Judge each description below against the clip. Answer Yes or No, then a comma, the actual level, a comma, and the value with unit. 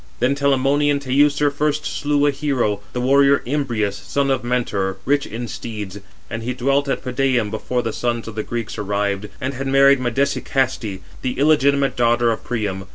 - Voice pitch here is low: Yes, low, 125 Hz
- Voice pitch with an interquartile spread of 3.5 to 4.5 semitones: Yes, average, 3.8 semitones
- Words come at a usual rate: Yes, average, 170 wpm